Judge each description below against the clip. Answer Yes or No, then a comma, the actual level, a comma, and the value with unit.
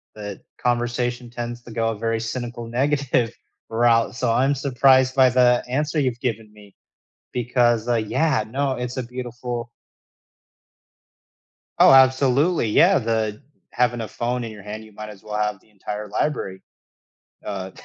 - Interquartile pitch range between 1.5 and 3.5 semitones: Yes, narrow, 2.6 semitones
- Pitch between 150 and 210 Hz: No, low, 120 Hz